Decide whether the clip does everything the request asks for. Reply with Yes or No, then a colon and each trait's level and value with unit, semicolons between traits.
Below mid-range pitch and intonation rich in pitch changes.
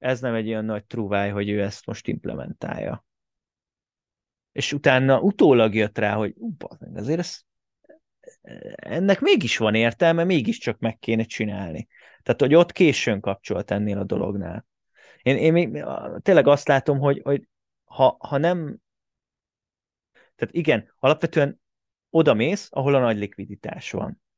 Yes: low, 120 Hz; wide, 7.5 semitones